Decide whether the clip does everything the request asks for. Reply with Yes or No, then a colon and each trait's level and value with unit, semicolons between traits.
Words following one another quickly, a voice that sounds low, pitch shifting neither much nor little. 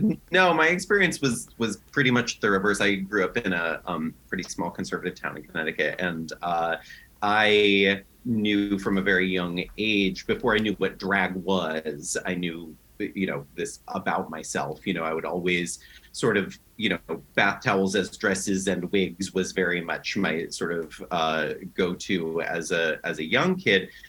No: average, 180 wpm; very low, 95 Hz; average, 3.4 semitones